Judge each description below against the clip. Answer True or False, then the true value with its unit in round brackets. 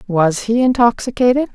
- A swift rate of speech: False (115 wpm)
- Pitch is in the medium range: False (230 Hz)